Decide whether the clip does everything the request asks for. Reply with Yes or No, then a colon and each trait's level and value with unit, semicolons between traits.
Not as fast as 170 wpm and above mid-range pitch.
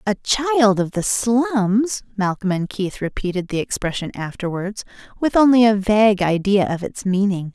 Yes: average, 160 wpm; high, 205 Hz